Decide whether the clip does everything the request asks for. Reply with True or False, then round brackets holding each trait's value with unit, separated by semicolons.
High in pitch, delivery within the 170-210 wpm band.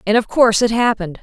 False (220 Hz; 245 wpm)